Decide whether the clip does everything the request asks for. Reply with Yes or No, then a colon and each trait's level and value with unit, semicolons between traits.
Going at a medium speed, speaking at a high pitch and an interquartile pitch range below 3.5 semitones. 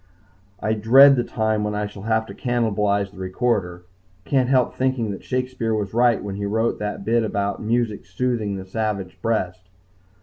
No: average, 175 wpm; low, 110 Hz; average, 2.9 semitones